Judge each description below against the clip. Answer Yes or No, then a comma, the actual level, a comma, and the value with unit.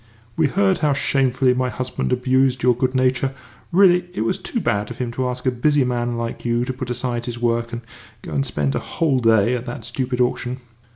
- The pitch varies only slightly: Yes, narrow, 2.0 semitones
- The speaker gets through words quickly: Yes, fast, 220 wpm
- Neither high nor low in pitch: No, low, 125 Hz